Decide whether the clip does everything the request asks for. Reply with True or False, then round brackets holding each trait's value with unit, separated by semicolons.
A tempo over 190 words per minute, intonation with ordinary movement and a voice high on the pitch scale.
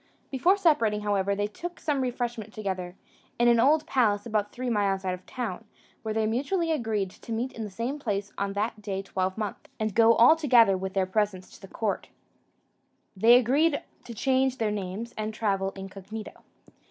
False (180 wpm; 3.8 semitones; 220 Hz)